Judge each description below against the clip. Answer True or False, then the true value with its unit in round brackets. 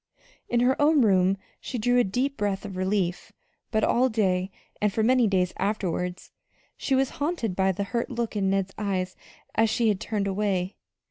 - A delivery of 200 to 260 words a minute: False (185 wpm)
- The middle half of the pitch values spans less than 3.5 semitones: False (4.0 semitones)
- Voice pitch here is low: False (205 Hz)